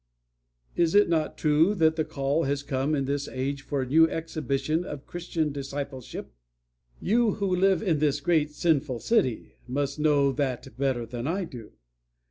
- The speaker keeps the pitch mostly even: No, average, 3.2 semitones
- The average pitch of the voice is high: No, medium, 145 Hz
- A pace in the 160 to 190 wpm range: Yes, average, 165 wpm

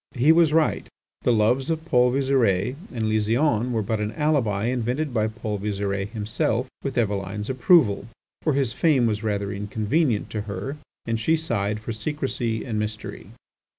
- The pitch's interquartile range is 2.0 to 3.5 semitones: No, average, 4.1 semitones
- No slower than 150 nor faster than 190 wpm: Yes, average, 160 wpm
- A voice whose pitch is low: Yes, low, 115 Hz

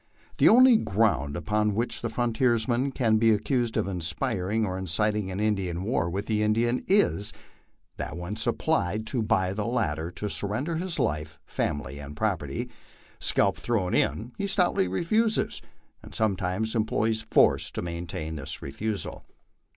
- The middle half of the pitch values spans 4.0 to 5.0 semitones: Yes, average, 4.6 semitones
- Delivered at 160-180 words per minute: No, average, 150 wpm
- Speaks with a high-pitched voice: No, low, 105 Hz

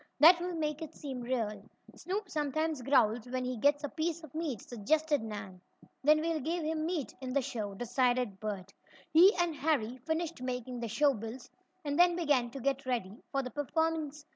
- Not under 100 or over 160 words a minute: No, average, 190 wpm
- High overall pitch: Yes, very high, 275 Hz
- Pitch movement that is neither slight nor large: Yes, average, 4.6 semitones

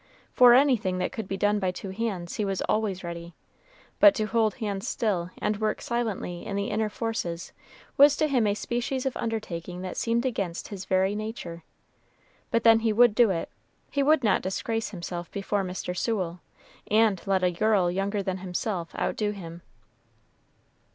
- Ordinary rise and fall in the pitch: Yes, average, 3.6 semitones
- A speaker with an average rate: Yes, average, 175 wpm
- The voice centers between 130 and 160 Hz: No, high, 205 Hz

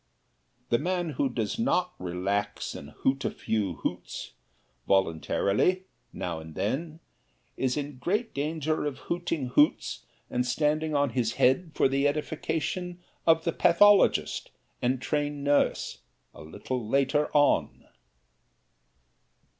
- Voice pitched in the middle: Yes, medium, 145 Hz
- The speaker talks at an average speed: No, slow, 120 wpm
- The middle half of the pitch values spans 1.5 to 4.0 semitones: No, average, 4.8 semitones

